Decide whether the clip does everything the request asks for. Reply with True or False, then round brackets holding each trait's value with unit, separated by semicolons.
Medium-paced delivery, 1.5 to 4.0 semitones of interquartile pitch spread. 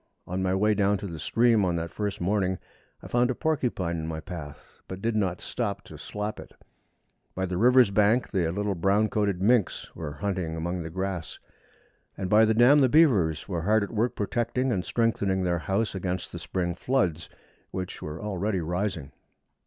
True (190 wpm; 3.7 semitones)